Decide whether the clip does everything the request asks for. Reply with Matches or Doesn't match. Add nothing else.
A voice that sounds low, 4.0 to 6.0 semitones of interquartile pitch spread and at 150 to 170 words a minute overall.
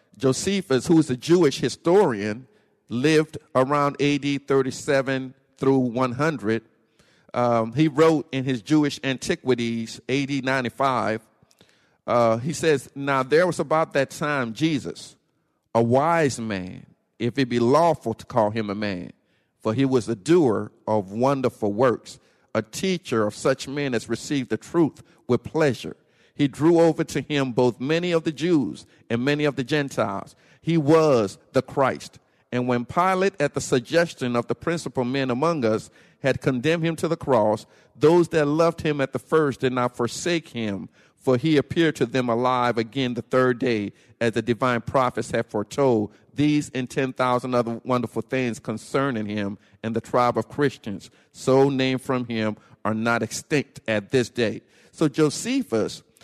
Matches